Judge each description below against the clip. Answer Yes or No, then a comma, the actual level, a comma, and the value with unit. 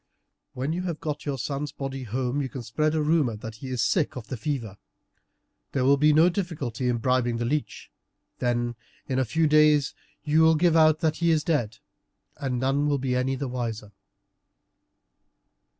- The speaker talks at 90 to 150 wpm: No, average, 185 wpm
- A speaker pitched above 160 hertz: No, low, 135 Hz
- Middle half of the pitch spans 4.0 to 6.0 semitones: No, average, 3.6 semitones